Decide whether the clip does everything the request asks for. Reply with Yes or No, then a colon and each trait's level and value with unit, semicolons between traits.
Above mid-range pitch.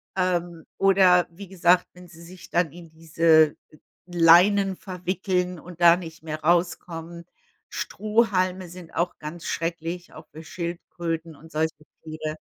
No: medium, 170 Hz